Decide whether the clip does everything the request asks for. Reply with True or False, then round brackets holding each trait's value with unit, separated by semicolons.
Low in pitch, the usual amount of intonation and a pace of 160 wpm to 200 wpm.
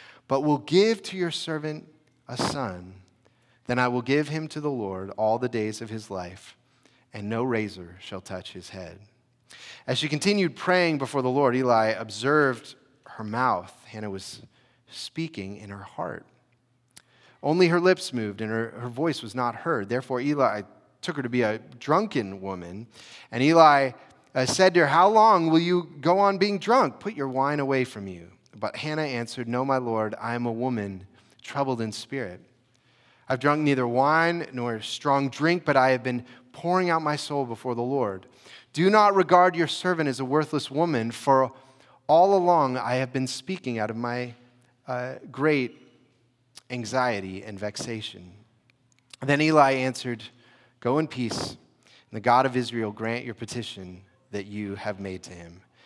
True (125 Hz; 4.5 semitones; 175 wpm)